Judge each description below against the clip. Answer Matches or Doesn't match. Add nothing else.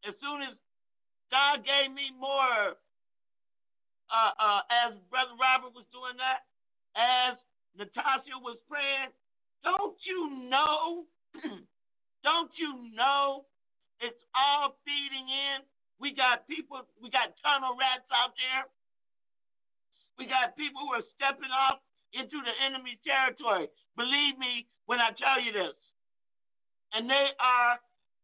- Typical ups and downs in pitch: Doesn't match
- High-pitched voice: Matches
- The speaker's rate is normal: Doesn't match